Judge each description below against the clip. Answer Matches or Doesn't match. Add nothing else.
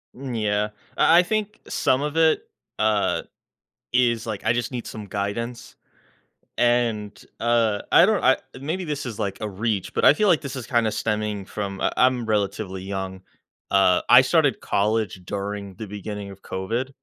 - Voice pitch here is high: Doesn't match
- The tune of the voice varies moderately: Matches